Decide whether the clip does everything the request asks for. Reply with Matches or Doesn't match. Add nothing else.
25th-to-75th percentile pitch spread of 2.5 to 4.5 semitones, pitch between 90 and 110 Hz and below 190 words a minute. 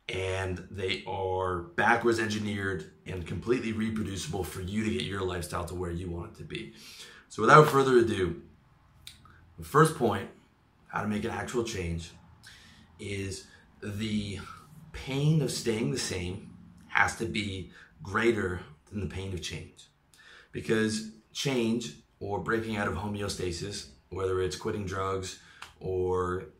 Matches